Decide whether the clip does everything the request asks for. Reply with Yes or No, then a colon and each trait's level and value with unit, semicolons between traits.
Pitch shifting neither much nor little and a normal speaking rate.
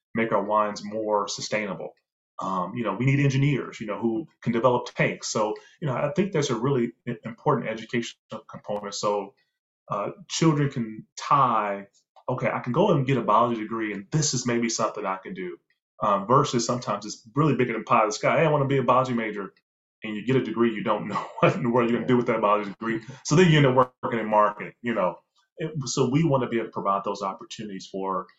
No: average, 3.9 semitones; fast, 230 wpm